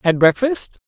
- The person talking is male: No, female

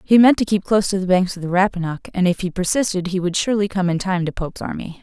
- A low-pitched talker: No, high, 190 Hz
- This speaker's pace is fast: Yes, fast, 285 wpm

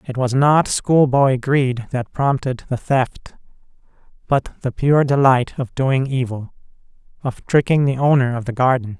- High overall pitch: No, low, 130 Hz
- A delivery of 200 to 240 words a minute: No, average, 155 wpm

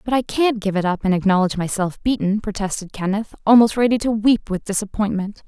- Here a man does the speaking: No, female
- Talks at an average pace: Yes, average, 195 wpm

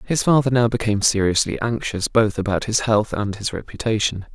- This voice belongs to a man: Yes, male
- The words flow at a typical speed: Yes, average, 180 wpm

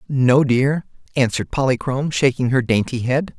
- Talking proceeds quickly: No, average, 140 wpm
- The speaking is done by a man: Yes, male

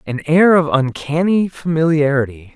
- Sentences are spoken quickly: No, slow, 115 wpm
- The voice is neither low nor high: Yes, medium, 155 Hz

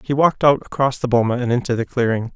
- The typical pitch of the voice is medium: No, low, 125 Hz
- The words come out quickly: Yes, fast, 255 wpm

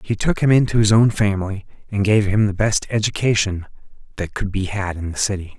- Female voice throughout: No, male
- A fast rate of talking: Yes, fast, 215 wpm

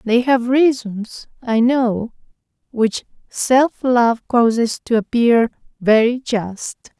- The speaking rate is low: Yes, slow, 110 wpm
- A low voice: No, high, 235 Hz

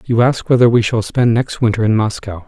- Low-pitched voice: Yes, low, 115 Hz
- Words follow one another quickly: Yes, fast, 245 wpm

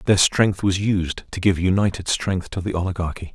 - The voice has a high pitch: No, very low, 95 Hz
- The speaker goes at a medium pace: Yes, average, 195 wpm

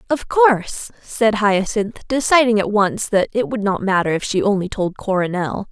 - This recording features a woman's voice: Yes, female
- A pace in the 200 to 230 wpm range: No, average, 180 wpm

